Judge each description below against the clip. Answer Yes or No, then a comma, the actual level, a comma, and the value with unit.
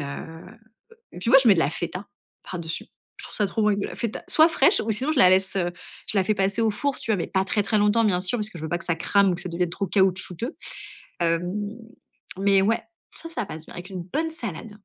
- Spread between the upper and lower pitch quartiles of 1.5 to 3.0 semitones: No, average, 3.8 semitones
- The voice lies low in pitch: No, high, 200 Hz